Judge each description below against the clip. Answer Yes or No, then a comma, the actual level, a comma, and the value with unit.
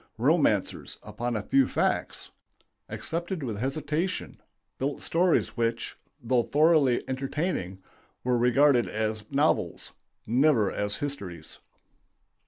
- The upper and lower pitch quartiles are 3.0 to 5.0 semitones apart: Yes, average, 4.7 semitones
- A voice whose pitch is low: Yes, low, 130 Hz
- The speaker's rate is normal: No, slow, 100 wpm